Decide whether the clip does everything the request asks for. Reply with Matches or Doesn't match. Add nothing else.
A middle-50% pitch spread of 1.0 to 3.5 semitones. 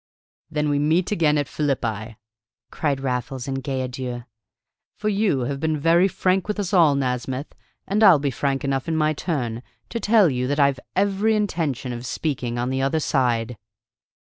Doesn't match